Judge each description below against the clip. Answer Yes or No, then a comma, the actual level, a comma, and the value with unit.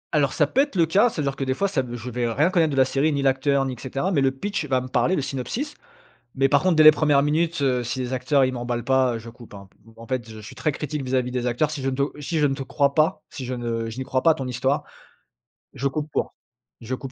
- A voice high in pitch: No, low, 135 Hz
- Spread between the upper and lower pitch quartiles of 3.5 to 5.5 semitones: No, average, 3.1 semitones